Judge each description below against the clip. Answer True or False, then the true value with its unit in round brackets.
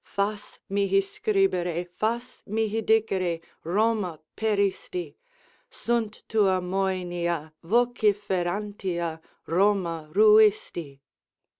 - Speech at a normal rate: False (70 wpm)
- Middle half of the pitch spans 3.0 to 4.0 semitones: True (3.5 semitones)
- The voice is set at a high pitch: True (195 Hz)